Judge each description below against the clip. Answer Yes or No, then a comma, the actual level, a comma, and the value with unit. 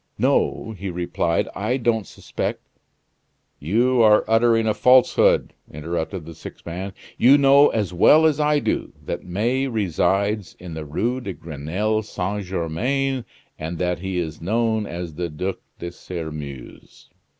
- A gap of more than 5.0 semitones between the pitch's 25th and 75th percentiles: Yes, wide, 5.5 semitones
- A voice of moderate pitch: No, low, 100 Hz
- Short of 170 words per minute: Yes, average, 150 wpm